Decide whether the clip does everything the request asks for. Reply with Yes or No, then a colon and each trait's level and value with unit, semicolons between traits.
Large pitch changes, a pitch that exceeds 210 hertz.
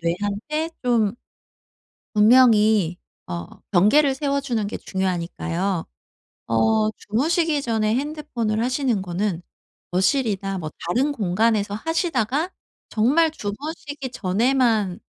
Yes: wide, 5.8 semitones; high, 220 Hz